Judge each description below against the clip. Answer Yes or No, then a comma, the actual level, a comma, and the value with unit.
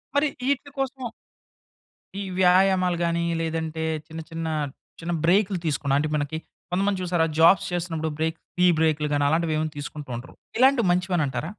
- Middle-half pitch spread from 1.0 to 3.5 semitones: Yes, average, 2.8 semitones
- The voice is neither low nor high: Yes, medium, 165 Hz